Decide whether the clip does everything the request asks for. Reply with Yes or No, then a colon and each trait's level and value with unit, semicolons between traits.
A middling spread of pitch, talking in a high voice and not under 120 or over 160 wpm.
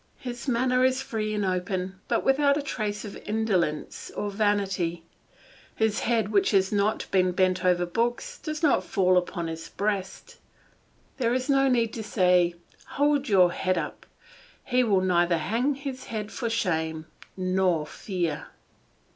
Yes: average, 4.9 semitones; high, 205 Hz; average, 155 wpm